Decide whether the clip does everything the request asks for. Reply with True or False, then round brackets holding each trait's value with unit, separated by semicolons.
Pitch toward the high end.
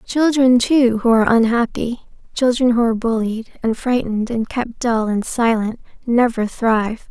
True (235 Hz)